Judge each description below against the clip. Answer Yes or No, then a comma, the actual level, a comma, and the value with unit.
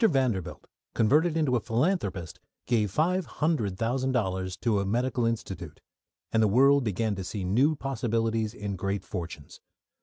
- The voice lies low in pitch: Yes, low, 115 Hz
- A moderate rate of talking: Yes, average, 150 wpm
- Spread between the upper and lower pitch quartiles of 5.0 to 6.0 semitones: Yes, average, 5.3 semitones